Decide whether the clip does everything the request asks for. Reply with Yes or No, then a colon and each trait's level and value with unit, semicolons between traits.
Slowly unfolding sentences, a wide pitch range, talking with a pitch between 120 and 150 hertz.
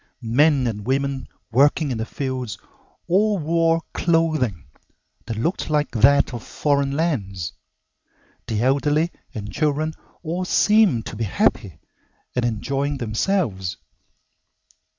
Yes: slow, 115 wpm; wide, 5.9 semitones; medium, 140 Hz